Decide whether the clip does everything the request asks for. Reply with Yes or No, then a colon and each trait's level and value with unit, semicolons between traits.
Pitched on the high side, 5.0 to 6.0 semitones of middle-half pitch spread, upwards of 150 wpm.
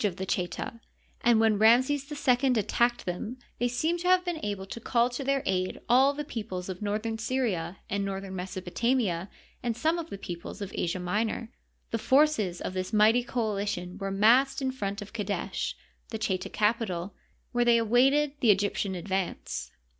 No: high, 220 Hz; average, 4.4 semitones; average, 175 wpm